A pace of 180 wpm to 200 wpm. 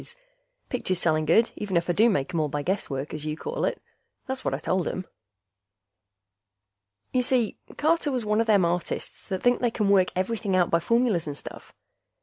Yes: average, 190 wpm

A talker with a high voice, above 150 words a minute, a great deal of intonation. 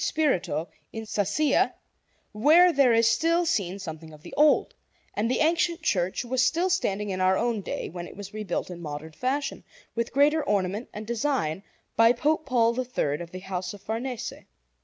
Yes: high, 225 Hz; average, 180 wpm; wide, 7.1 semitones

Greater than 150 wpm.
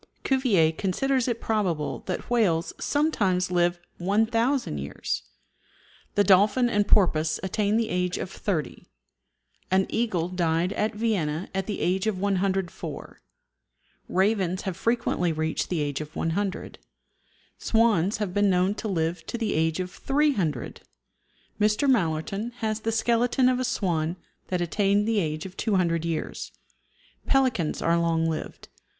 No: average, 140 wpm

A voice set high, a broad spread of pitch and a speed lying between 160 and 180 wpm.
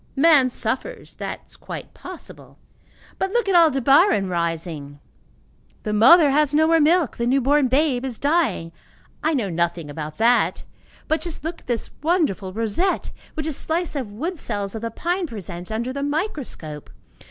Yes: very high, 265 Hz; wide, 7.6 semitones; average, 165 wpm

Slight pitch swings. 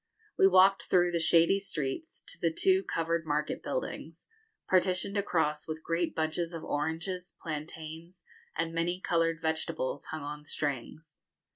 Yes: narrow, 2.3 semitones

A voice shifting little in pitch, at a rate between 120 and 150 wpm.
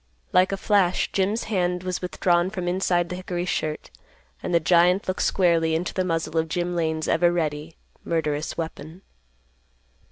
No: narrow, 2.0 semitones; average, 160 wpm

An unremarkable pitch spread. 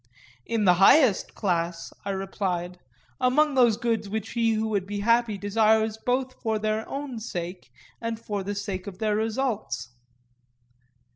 Yes: average, 3.0 semitones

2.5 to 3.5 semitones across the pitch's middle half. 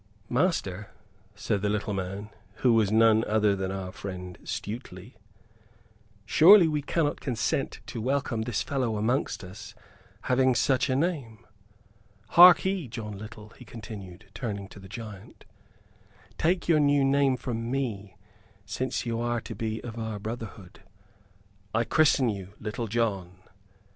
No: average, 4.1 semitones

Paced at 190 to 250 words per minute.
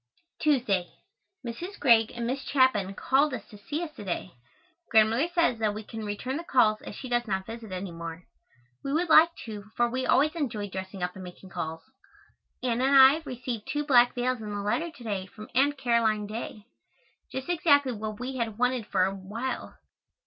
Yes: average, 195 wpm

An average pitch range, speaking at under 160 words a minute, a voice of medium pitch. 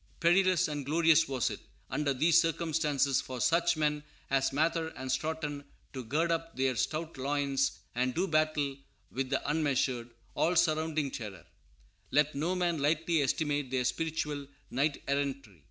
Yes: average, 3.1 semitones; average, 150 wpm; medium, 150 Hz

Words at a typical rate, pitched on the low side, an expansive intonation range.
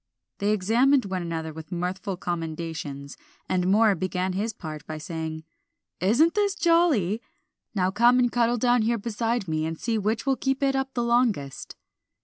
No: average, 165 wpm; high, 205 Hz; wide, 6.3 semitones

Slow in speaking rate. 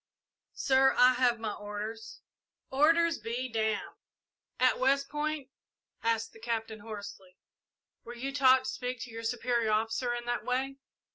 No: average, 145 wpm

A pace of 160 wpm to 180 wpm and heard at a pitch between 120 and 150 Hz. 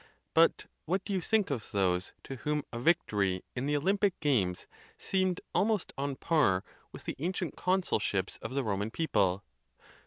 Yes: average, 175 wpm; medium, 140 Hz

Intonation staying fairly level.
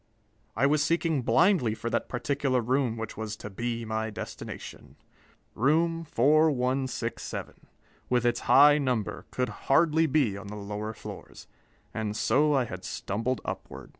No: average, 4.8 semitones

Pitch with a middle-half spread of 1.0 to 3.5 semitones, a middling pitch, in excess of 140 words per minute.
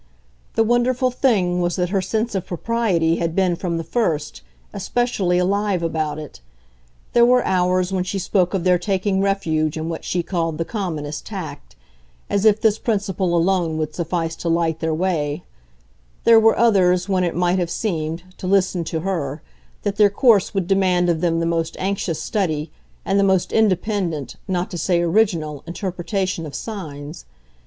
Yes: average, 3.2 semitones; medium, 180 Hz; average, 175 wpm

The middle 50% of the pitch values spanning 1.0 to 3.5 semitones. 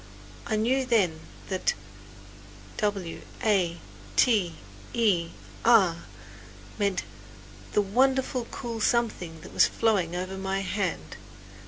No: average, 4.2 semitones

